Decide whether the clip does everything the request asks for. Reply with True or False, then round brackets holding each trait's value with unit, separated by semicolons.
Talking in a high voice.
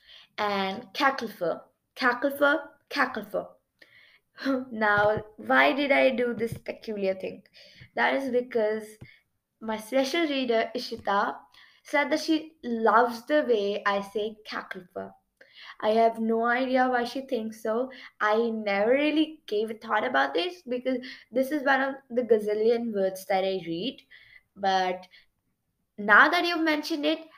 True (230 Hz)